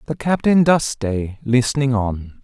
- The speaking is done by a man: Yes, male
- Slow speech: No, average, 150 wpm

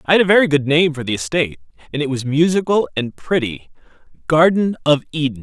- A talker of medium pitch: Yes, medium, 150 Hz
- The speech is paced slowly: No, average, 200 wpm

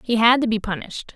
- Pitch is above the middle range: Yes, high, 225 Hz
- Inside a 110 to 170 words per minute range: No, fast, 260 wpm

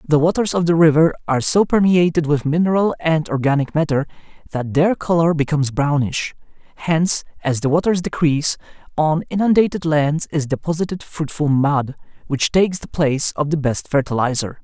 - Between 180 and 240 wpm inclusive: No, average, 155 wpm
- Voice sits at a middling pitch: Yes, medium, 155 Hz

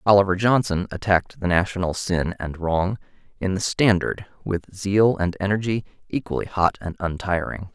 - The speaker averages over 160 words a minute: No, average, 145 wpm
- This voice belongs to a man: Yes, male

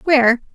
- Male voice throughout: No, female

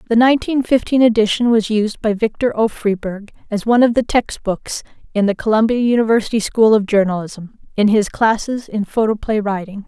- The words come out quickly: No, average, 175 wpm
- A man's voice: No, female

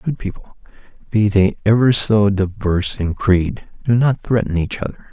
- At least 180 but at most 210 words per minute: No, average, 165 wpm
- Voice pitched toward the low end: Yes, low, 105 Hz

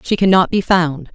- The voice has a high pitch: No, medium, 175 Hz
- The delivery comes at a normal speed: No, fast, 210 wpm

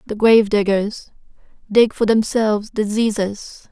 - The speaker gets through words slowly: Yes, slow, 115 wpm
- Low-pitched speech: No, high, 215 Hz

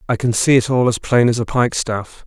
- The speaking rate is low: No, fast, 265 wpm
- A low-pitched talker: Yes, low, 120 Hz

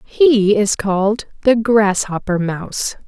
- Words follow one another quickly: No, slow, 115 wpm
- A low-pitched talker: No, high, 210 Hz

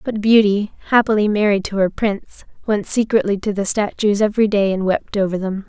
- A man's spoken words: No, female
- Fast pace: No, average, 190 wpm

